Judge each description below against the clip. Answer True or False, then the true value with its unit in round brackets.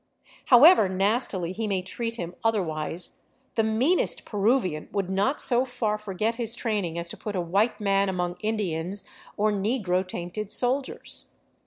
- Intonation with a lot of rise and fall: False (3.9 semitones)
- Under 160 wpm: True (150 wpm)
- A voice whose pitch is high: True (205 Hz)